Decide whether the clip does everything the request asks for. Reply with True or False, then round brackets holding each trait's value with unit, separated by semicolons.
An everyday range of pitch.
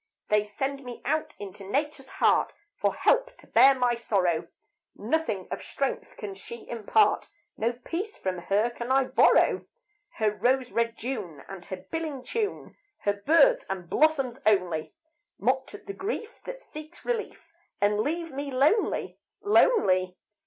False (7.7 semitones)